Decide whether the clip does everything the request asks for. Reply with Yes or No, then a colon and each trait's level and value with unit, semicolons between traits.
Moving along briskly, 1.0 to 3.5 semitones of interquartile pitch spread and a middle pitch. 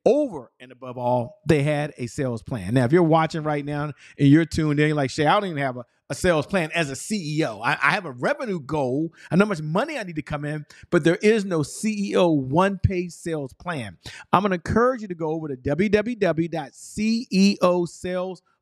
No: fast, 215 wpm; average, 4.5 semitones; medium, 160 Hz